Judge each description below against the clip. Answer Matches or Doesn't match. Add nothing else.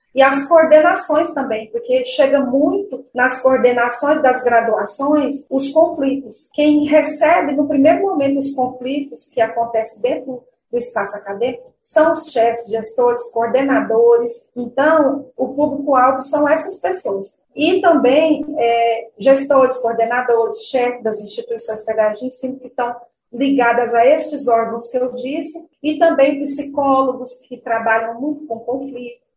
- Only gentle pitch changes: Doesn't match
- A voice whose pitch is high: Matches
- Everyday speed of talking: Matches